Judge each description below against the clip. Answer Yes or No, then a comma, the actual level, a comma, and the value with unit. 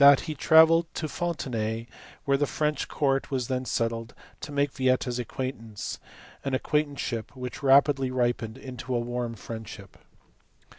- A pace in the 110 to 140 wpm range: Yes, slow, 135 wpm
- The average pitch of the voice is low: Yes, low, 130 Hz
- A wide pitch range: No, average, 3.3 semitones